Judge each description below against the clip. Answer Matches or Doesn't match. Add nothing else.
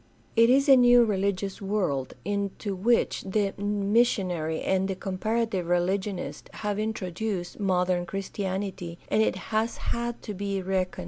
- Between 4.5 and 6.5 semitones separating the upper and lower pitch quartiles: Doesn't match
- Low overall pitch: Doesn't match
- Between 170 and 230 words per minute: Doesn't match